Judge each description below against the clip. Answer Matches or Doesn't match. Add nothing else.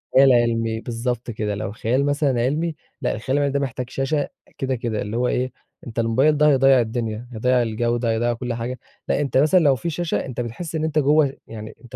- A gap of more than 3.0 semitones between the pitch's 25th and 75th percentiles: Matches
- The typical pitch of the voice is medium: Doesn't match